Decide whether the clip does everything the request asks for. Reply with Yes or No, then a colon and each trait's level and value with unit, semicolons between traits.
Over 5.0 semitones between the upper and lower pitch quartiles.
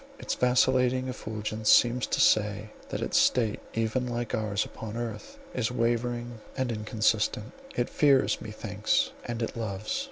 No: narrow, 2.4 semitones